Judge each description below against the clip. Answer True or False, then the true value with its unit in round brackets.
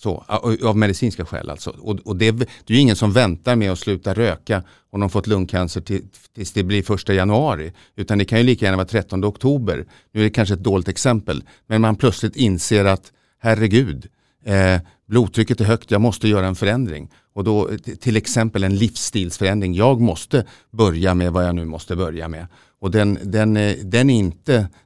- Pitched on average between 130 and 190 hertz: False (105 Hz)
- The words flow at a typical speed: False (205 wpm)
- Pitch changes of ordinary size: True (3.4 semitones)